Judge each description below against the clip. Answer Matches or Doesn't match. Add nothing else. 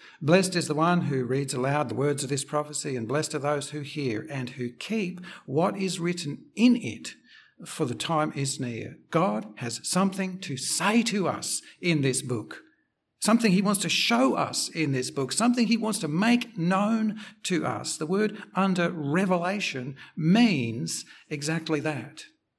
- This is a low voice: Doesn't match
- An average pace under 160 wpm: Doesn't match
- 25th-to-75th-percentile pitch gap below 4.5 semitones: Doesn't match